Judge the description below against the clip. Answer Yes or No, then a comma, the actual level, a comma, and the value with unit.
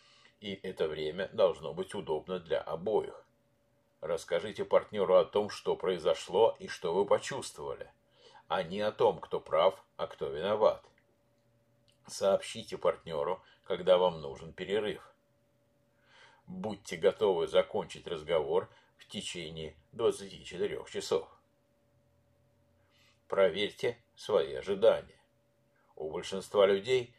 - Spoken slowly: Yes, slow, 105 wpm